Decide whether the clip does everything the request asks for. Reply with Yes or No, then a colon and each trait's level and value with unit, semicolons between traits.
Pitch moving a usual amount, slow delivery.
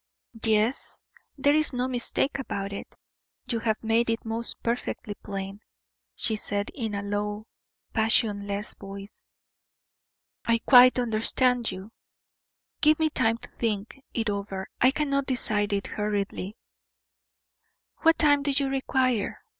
Yes: average, 3.8 semitones; slow, 130 wpm